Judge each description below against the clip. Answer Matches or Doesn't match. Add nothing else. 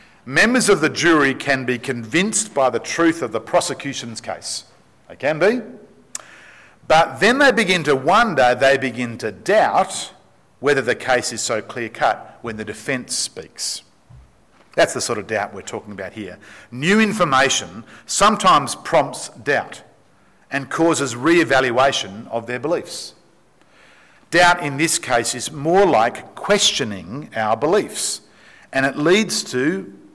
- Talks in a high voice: Doesn't match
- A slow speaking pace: Doesn't match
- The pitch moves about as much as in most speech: Doesn't match